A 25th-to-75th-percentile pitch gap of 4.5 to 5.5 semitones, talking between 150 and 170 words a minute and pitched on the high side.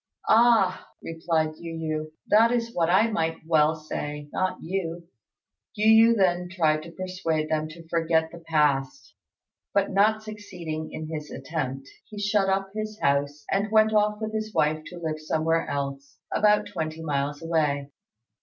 No: average, 4.8 semitones; average, 160 wpm; medium, 165 Hz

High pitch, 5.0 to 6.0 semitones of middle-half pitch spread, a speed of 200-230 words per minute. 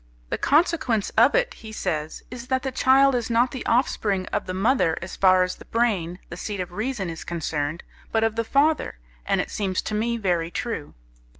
Yes: high, 220 Hz; wide, 5.5 semitones; fast, 205 wpm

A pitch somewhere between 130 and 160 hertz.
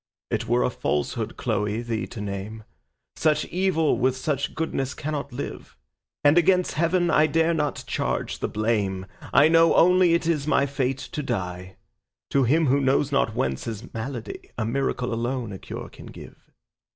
Yes: low, 135 Hz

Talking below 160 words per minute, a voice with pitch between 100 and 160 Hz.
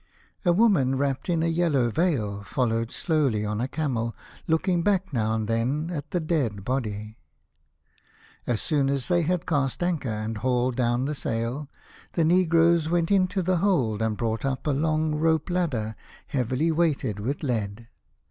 No: average, 165 wpm; medium, 140 Hz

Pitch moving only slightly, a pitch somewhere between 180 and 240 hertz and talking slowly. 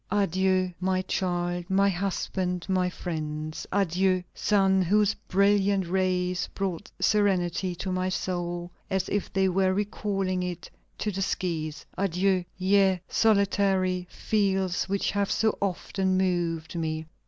Yes: narrow, 1.7 semitones; medium, 185 Hz; slow, 125 wpm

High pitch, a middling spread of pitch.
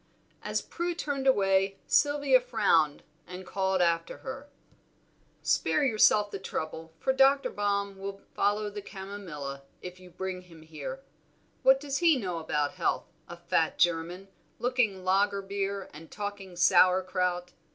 Yes: high, 195 Hz; average, 3.7 semitones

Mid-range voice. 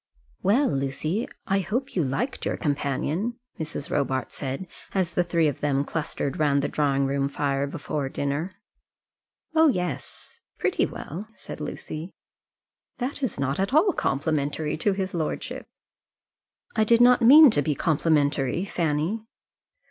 Yes: medium, 155 Hz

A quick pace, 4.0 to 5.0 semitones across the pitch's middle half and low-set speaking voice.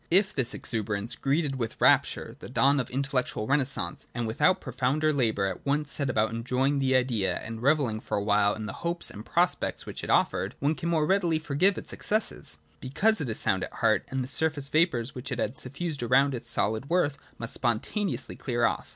Yes: fast, 210 wpm; average, 4.7 semitones; low, 130 Hz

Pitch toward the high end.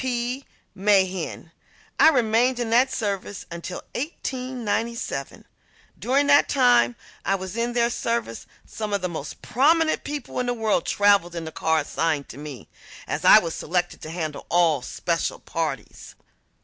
Yes: high, 210 Hz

